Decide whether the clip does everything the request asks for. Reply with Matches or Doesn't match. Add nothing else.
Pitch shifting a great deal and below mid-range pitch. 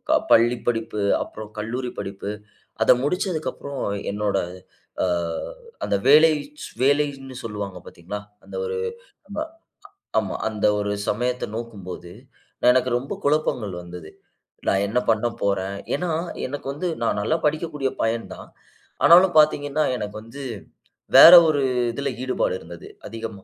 Matches